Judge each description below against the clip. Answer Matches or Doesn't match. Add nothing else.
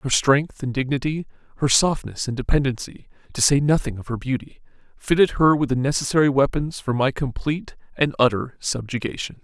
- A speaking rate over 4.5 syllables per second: Matches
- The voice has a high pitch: Doesn't match